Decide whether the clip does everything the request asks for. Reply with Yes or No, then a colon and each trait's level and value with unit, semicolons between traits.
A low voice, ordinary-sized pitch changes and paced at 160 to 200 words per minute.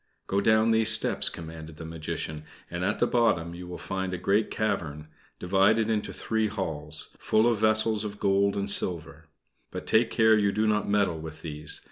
Yes: low, 100 Hz; average, 4.9 semitones; average, 185 wpm